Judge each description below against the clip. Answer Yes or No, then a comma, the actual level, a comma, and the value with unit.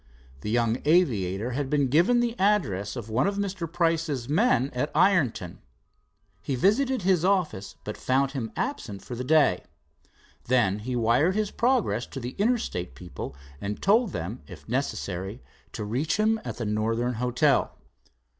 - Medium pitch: No, low, 130 Hz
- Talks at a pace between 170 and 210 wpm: No, average, 155 wpm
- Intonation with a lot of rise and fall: Yes, wide, 8.6 semitones